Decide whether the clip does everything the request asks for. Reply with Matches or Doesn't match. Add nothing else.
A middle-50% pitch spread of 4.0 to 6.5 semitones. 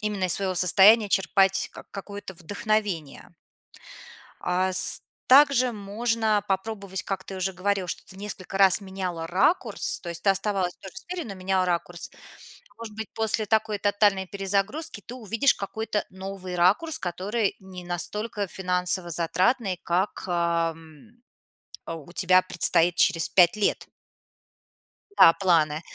Doesn't match